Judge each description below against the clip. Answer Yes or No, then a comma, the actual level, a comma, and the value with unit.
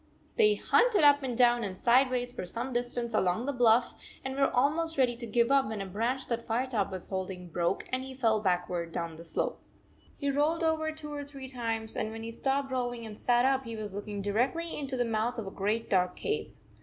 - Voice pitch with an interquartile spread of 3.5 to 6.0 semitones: Yes, average, 4.0 semitones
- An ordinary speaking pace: No, fast, 225 wpm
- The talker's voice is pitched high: Yes, high, 240 Hz